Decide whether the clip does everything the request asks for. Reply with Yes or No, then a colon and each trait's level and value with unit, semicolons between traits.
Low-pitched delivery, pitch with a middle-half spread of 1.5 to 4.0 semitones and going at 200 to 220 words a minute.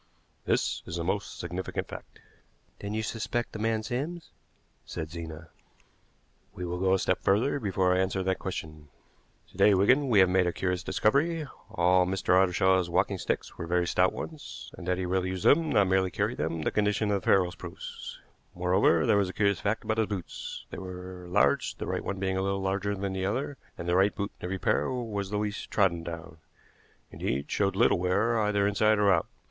Yes: very low, 95 Hz; narrow, 2.5 semitones; fast, 205 wpm